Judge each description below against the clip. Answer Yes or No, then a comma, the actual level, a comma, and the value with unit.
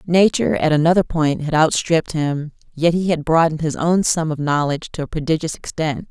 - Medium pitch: Yes, medium, 160 Hz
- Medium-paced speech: Yes, average, 195 wpm